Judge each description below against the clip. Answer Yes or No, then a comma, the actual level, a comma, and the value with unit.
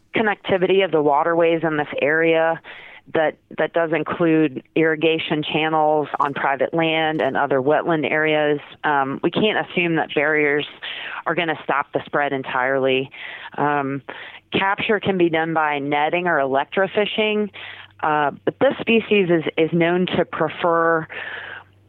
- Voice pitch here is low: No, medium, 160 Hz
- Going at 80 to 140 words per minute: Yes, slow, 135 wpm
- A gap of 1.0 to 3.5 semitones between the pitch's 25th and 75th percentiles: Yes, narrow, 2.6 semitones